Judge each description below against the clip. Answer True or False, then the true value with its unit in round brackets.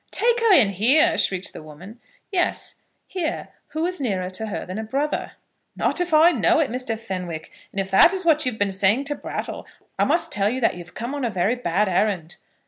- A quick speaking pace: True (220 wpm)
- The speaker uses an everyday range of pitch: False (8.2 semitones)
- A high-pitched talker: True (225 Hz)